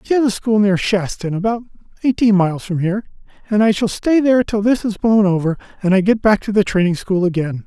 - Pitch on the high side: Yes, high, 200 Hz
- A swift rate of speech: Yes, fast, 225 wpm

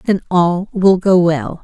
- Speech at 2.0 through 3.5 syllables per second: Yes, 3.4 syllables/s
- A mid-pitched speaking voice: Yes, medium, 175 Hz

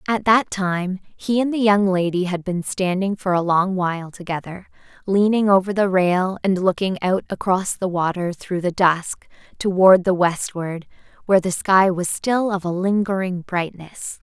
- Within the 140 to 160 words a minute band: No, average, 170 wpm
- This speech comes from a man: No, female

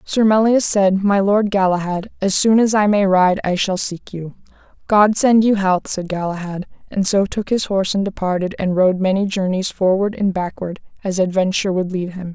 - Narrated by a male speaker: No, female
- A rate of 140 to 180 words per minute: No, average, 200 wpm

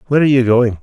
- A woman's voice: No, male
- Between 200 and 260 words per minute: No, fast, 290 wpm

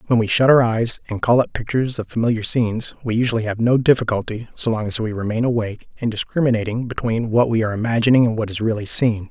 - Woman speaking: No, male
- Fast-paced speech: Yes, fast, 225 wpm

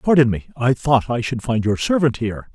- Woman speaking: No, male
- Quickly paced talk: Yes, fast, 235 wpm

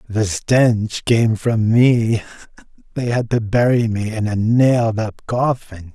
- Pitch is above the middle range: No, low, 115 Hz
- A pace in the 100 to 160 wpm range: Yes, average, 150 wpm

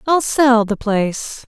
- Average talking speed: Yes, average, 160 wpm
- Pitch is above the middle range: Yes, high, 240 Hz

